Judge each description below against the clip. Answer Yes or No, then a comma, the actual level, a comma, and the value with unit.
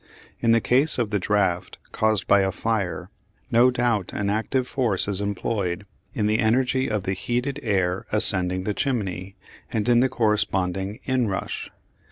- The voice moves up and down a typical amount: Yes, average, 3.8 semitones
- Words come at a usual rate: Yes, average, 160 wpm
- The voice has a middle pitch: No, low, 105 Hz